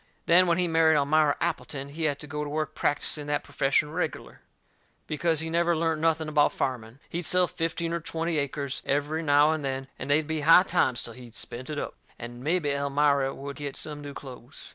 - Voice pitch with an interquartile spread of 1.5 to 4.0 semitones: Yes, narrow, 2.5 semitones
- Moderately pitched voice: Yes, medium, 150 Hz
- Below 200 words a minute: No, fast, 205 wpm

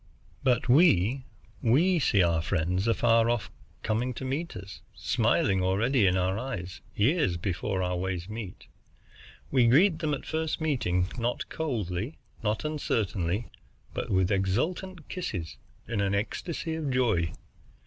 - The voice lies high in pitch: No, low, 115 Hz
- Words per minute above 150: No, average, 140 wpm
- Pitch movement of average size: No, wide, 6.7 semitones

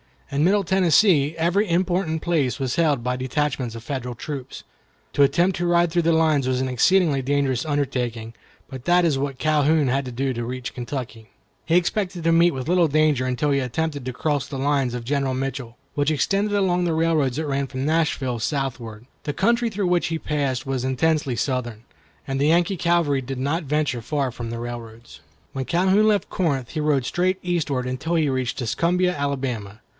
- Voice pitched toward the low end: No, medium, 145 Hz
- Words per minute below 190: No, average, 195 wpm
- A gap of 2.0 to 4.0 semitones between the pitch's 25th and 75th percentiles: No, average, 4.6 semitones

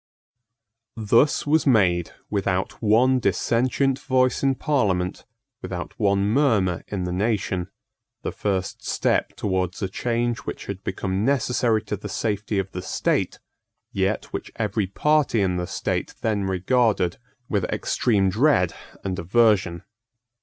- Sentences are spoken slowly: Yes, slow, 130 wpm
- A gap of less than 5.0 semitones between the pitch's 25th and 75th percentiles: Yes, average, 4.3 semitones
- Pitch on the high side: No, low, 105 Hz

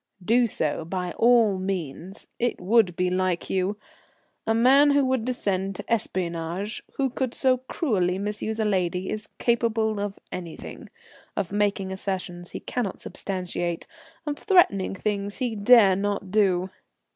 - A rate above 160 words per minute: No, average, 145 wpm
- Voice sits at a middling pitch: No, high, 200 Hz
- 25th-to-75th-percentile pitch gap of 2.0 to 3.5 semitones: No, average, 3.9 semitones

